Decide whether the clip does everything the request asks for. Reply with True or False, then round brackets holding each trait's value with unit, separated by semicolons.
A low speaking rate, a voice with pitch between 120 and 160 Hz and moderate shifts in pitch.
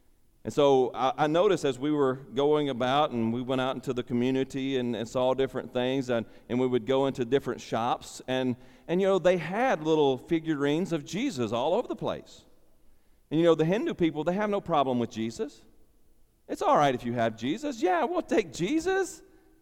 False (205 wpm; 135 Hz; 5.0 semitones)